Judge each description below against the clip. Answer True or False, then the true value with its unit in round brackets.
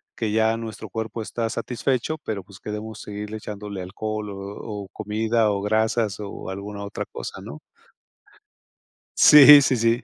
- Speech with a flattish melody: True (1.8 semitones)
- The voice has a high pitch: False (110 Hz)